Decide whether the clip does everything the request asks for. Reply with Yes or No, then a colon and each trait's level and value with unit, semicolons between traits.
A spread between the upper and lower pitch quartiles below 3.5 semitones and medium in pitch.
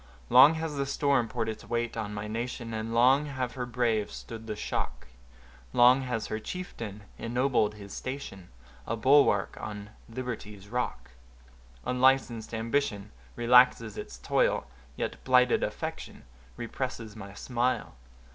No: average, 3.1 semitones; low, 115 Hz